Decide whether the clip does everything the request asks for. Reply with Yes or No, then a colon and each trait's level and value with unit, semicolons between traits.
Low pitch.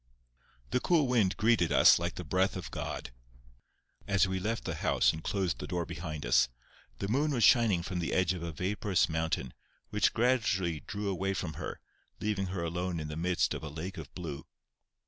Yes: very low, 90 Hz